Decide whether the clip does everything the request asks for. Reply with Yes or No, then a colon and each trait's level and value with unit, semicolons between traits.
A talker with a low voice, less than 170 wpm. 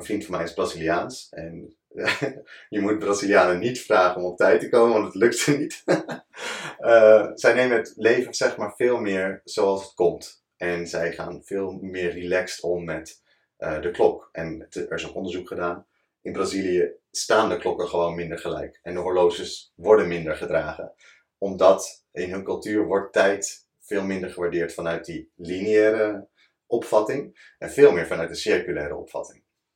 No: very low, 95 Hz; average, 175 wpm